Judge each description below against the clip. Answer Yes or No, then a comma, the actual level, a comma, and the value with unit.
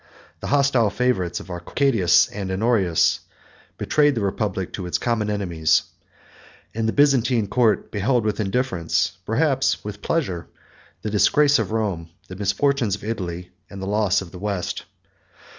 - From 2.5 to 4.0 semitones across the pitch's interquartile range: No, average, 4.7 semitones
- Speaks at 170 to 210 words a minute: No, average, 145 wpm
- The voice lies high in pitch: No, low, 105 Hz